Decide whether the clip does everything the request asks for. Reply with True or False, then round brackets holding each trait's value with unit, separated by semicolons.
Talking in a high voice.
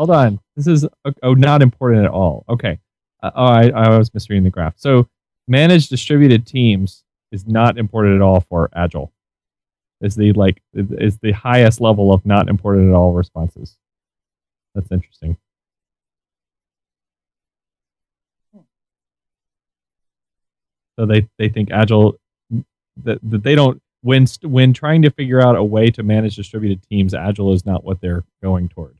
False (105 Hz)